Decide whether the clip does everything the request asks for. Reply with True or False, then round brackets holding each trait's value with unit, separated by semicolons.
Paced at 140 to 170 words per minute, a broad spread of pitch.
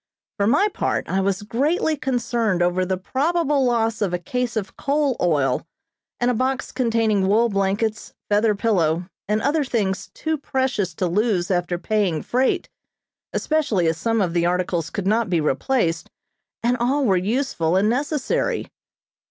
True (160 wpm; 5.7 semitones)